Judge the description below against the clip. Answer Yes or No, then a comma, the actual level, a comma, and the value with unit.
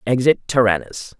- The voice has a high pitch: No, low, 115 Hz